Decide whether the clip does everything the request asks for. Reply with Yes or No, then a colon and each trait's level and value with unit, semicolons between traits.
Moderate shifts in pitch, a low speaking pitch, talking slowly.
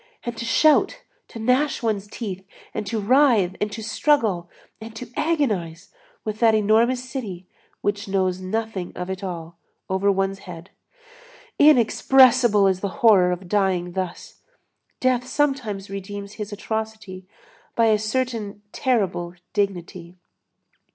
No: average, 3.8 semitones; high, 210 Hz; slow, 130 wpm